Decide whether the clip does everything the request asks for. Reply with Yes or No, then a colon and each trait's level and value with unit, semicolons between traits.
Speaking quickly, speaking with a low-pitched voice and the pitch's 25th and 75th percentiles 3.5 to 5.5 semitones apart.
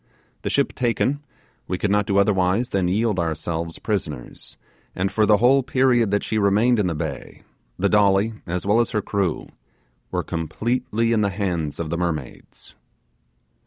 No: average, 165 wpm; low, 100 Hz; average, 4.3 semitones